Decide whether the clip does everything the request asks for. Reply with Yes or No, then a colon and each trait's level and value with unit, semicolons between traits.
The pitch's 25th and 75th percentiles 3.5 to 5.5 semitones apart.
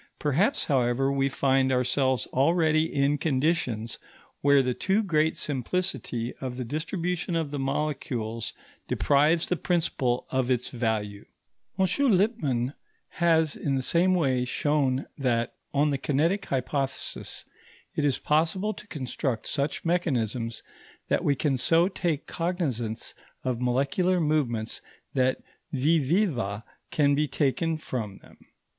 Yes: average, 4.4 semitones